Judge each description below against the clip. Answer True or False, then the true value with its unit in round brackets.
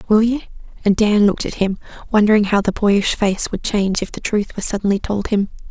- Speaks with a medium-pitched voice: False (205 Hz)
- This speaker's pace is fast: True (220 wpm)